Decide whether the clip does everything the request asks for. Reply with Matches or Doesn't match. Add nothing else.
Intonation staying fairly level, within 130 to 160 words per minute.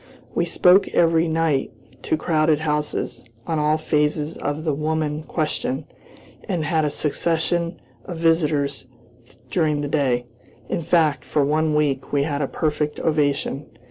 Matches